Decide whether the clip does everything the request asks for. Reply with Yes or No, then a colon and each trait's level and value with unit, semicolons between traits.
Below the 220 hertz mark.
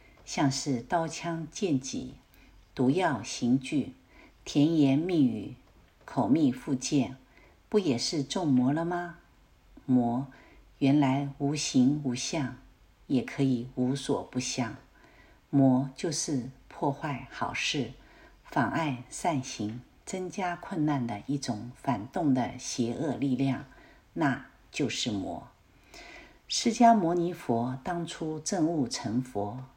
Yes: medium, 140 Hz